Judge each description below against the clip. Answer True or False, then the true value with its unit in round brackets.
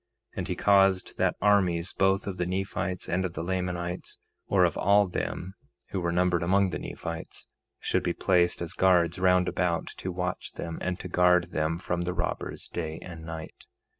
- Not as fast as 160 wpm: False (185 wpm)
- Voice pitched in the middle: False (90 Hz)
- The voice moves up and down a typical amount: False (1.5 semitones)